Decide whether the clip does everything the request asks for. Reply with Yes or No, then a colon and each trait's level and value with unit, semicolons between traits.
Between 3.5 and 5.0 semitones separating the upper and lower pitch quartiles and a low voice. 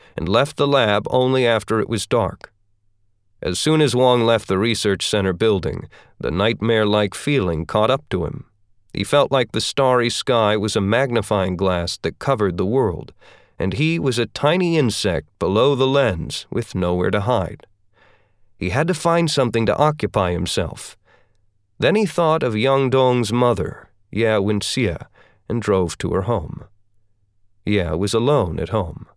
Yes: average, 4.6 semitones; low, 110 Hz